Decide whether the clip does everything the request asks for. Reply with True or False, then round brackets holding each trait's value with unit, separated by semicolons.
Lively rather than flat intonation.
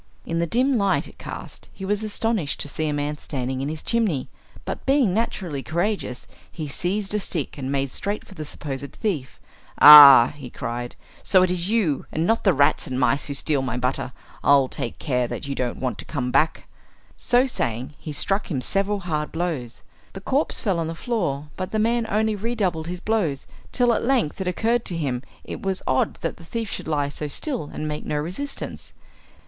True (6.8 semitones)